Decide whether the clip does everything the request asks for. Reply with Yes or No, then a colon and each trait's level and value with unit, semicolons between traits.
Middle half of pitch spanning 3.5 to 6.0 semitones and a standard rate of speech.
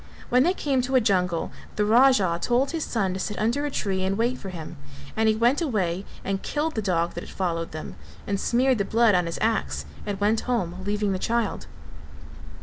No: average, 4.9 semitones; fast, 215 wpm